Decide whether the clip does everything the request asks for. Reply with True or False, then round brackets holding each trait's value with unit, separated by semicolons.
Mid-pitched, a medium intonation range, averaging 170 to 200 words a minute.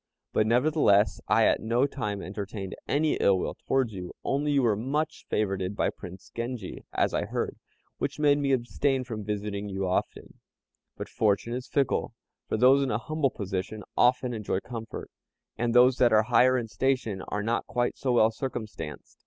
False (115 Hz; 4.2 semitones; 180 wpm)